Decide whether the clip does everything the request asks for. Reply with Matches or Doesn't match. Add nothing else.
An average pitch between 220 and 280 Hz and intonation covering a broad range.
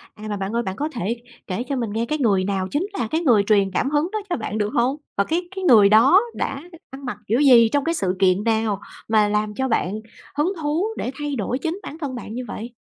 Matches